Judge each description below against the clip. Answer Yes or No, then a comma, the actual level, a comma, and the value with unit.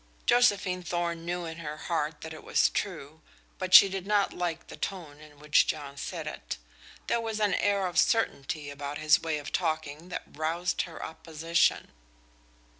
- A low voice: No, medium, 165 Hz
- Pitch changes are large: No, average, 3.3 semitones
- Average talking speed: Yes, average, 175 wpm